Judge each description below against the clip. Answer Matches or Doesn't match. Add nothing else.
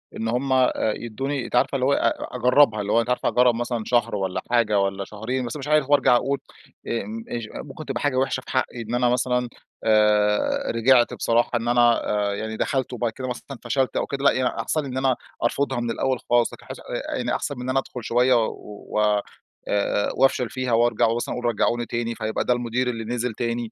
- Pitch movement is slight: Matches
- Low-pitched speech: Matches